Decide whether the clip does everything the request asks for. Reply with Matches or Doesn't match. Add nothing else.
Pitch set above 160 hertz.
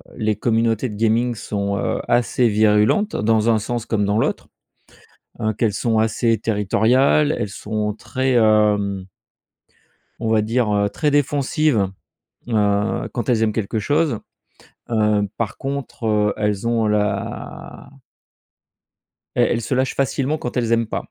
Doesn't match